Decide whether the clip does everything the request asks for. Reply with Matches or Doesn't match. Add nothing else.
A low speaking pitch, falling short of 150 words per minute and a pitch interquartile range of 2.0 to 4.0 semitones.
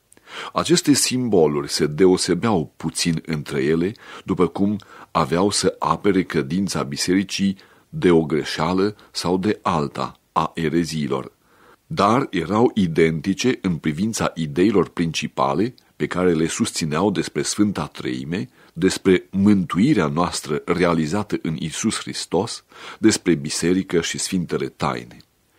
Matches